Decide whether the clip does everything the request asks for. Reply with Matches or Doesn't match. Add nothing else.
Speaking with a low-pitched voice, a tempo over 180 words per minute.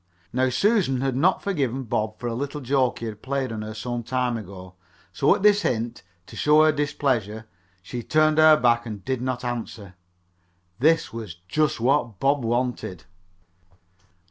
Doesn't match